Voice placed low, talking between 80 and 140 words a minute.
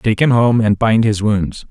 No: low, 110 Hz; fast, 245 wpm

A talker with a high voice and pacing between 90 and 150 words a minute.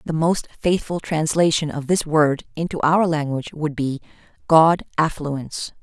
No: medium, 155 Hz; average, 145 wpm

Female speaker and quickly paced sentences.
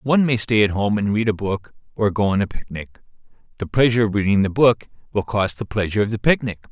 No: male; fast, 240 wpm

